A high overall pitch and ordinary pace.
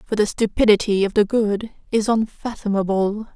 Yes: high, 210 Hz; average, 145 wpm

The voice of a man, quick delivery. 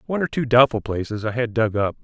Yes: male; fast, 265 wpm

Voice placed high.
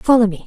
Yes: high, 220 Hz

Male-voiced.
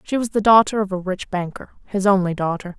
No: female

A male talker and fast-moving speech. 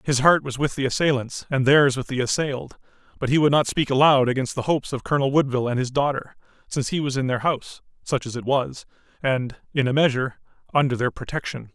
Yes: male; fast, 220 wpm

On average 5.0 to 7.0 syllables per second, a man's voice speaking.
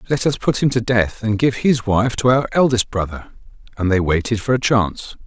Yes: 5.3 syllables/s; male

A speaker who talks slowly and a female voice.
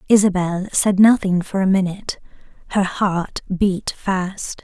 Yes: slow, 130 wpm; female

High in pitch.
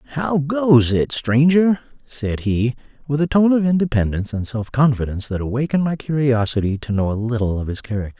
No: low, 130 Hz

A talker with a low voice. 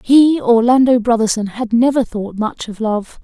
No: high, 235 Hz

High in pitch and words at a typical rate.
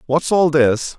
No: medium, 150 Hz; average, 180 wpm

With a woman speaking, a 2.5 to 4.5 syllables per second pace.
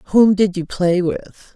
Yes: female; 4.3 syllables/s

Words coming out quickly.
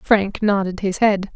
No: average, 175 wpm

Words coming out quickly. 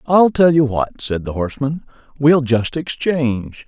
No: average, 165 wpm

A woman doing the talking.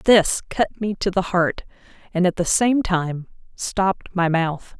Yes: female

